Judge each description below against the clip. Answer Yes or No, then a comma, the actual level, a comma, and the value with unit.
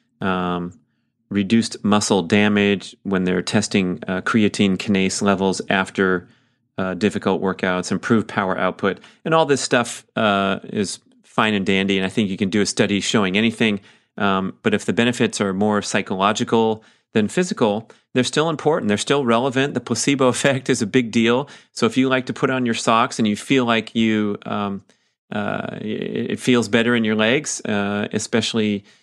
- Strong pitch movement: No, average, 3.5 semitones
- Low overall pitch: Yes, low, 110 Hz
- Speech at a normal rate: Yes, average, 175 wpm